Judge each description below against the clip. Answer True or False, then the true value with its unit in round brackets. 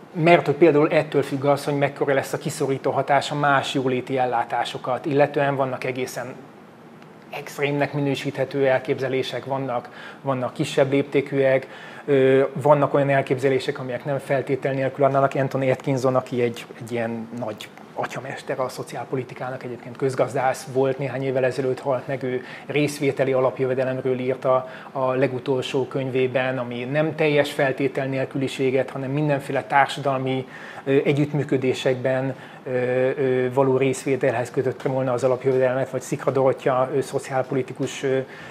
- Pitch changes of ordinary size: False (1.4 semitones)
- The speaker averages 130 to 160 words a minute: False (120 wpm)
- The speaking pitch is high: False (135 Hz)